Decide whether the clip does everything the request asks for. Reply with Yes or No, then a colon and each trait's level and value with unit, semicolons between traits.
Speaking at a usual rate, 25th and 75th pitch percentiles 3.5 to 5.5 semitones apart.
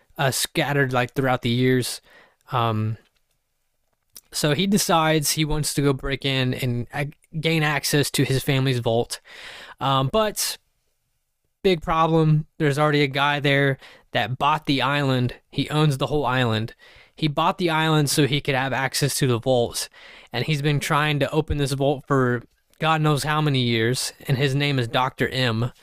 No: average, 170 wpm; average, 3.0 semitones